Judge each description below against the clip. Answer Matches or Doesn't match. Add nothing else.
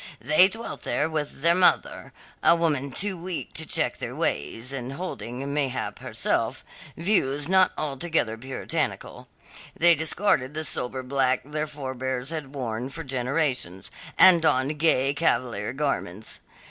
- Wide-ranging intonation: Doesn't match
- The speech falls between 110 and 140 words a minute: Matches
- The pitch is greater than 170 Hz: Doesn't match